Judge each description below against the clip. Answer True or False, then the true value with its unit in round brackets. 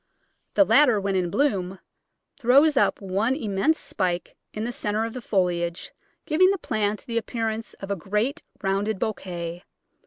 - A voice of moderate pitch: False (210 Hz)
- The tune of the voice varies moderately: True (4.4 semitones)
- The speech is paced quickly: False (155 wpm)